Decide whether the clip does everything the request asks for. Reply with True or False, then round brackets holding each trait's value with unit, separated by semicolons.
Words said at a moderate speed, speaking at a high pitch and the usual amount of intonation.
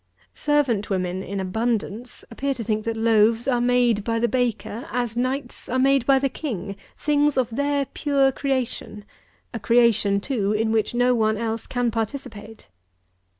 True (160 wpm; 235 Hz; 3.2 semitones)